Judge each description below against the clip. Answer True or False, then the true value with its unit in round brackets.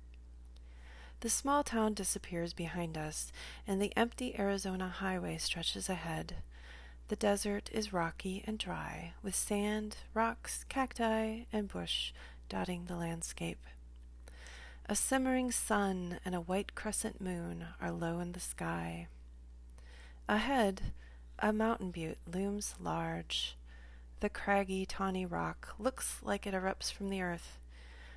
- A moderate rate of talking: False (125 wpm)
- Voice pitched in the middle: True (180 Hz)